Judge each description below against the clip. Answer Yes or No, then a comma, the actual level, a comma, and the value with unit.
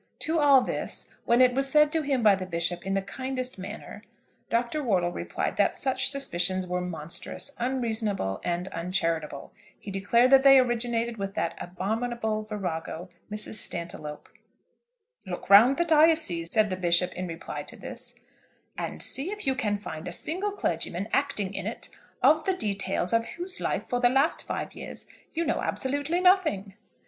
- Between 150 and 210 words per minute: Yes, average, 170 wpm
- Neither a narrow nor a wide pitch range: No, wide, 6.8 semitones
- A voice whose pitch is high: Yes, high, 220 Hz